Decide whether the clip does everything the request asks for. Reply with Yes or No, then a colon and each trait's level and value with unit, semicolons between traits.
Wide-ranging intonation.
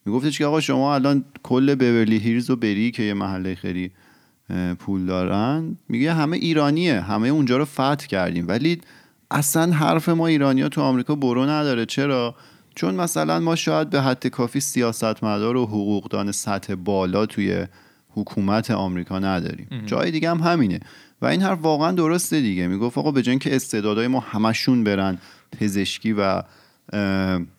Yes: wide, 6.2 semitones